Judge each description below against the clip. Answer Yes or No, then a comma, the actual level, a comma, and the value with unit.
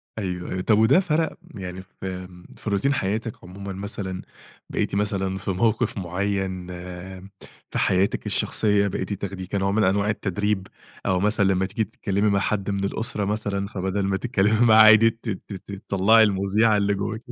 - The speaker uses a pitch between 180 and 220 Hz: No, low, 100 Hz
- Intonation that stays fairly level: Yes, narrow, 2.0 semitones